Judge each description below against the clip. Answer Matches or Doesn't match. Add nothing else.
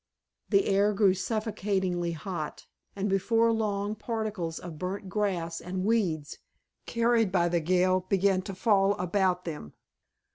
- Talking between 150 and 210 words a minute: Doesn't match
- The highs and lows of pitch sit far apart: Doesn't match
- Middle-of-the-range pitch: Doesn't match